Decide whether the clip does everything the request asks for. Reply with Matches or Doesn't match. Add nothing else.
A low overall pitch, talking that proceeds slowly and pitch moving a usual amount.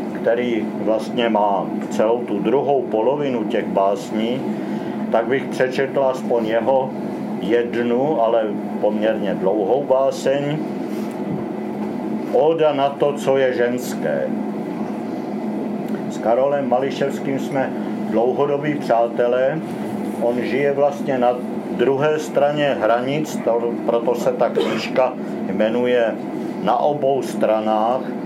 Matches